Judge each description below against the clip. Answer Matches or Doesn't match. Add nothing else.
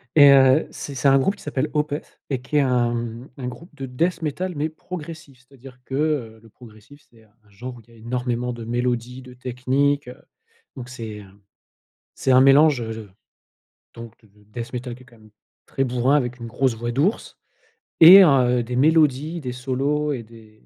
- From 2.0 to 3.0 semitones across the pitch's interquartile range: Doesn't match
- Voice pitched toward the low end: Matches